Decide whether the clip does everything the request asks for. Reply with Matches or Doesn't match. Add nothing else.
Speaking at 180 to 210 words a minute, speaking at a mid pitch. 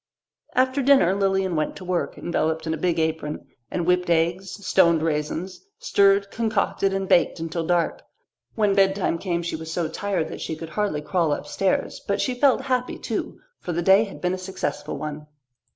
Matches